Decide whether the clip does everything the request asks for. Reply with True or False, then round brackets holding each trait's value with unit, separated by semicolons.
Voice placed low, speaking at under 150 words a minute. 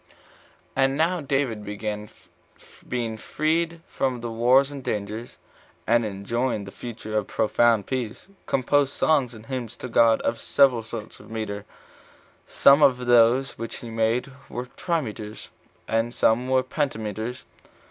True (120 Hz; 140 wpm)